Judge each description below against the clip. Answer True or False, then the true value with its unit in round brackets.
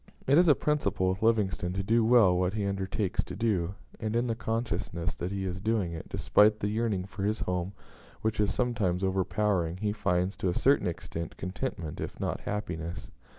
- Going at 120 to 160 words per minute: False (195 wpm)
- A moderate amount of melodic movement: True (3.6 semitones)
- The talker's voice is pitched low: True (100 Hz)